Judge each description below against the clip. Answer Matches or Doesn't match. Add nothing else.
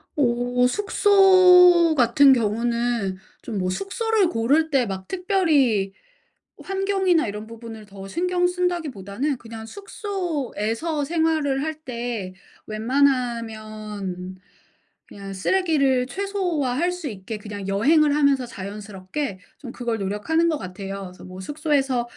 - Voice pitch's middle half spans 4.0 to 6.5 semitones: Doesn't match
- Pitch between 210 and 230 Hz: Doesn't match